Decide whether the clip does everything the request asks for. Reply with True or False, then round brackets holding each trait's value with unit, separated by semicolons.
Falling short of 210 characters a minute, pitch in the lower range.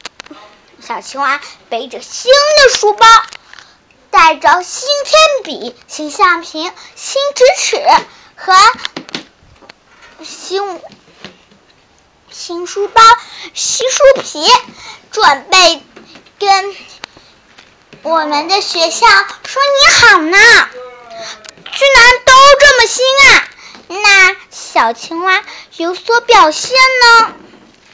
False (120 characters per minute; 355 Hz)